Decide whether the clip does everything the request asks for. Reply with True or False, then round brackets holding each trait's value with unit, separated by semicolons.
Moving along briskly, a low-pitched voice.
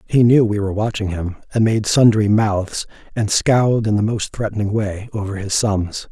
False (195 wpm; 105 Hz)